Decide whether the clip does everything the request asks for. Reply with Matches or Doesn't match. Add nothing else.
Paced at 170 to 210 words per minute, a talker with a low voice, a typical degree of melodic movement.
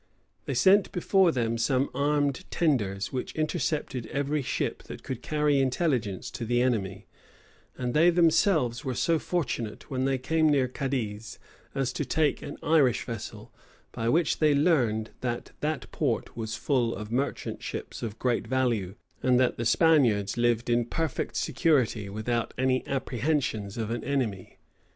Doesn't match